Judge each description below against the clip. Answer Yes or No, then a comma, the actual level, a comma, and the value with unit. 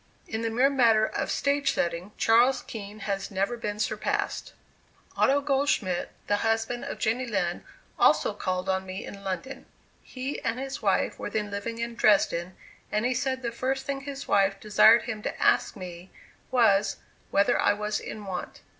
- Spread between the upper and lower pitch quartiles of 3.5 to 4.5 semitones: Yes, average, 4.2 semitones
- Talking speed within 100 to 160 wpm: No, average, 170 wpm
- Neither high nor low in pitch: No, high, 220 Hz